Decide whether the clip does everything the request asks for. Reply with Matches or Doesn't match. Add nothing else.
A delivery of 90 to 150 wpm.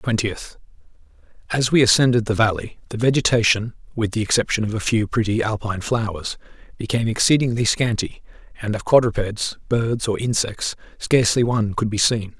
Matches